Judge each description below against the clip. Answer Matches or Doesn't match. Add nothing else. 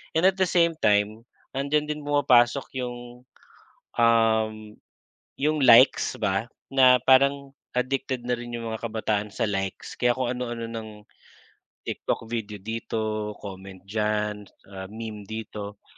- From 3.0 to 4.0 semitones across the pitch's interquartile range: Matches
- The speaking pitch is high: Doesn't match